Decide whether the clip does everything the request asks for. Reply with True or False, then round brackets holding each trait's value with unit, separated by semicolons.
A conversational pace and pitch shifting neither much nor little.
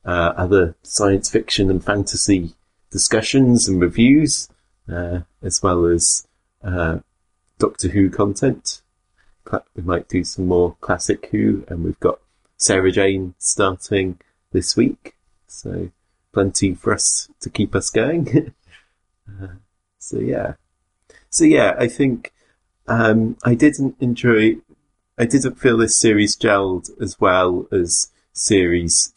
False (125 wpm; 3.7 semitones)